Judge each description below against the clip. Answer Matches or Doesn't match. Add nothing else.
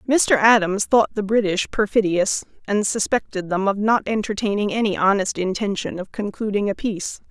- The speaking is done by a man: Doesn't match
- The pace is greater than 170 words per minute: Doesn't match